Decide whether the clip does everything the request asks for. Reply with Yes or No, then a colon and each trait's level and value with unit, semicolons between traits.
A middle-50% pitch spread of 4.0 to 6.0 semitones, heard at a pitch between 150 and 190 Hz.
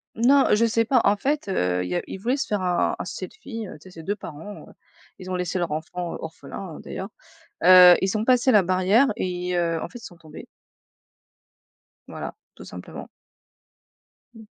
Yes: average, 4.5 semitones; medium, 185 Hz